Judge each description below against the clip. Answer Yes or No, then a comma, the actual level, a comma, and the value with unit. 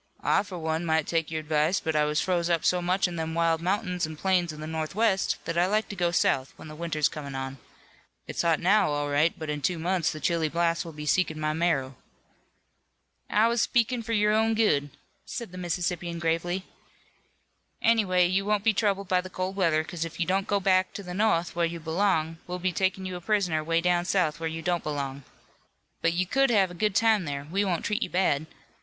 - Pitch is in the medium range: Yes, medium, 175 Hz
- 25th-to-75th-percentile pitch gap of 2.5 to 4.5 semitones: Yes, average, 3.1 semitones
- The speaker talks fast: Yes, fast, 225 wpm